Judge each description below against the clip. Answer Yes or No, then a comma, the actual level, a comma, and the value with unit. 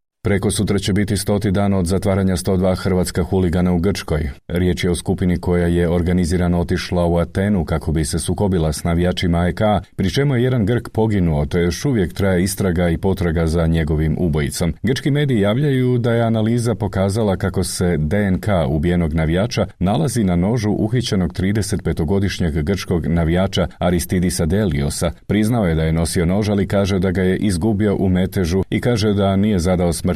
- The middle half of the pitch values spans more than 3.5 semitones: No, average, 2.8 semitones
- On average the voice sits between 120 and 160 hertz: No, very low, 95 Hz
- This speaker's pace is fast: Yes, fast, 175 wpm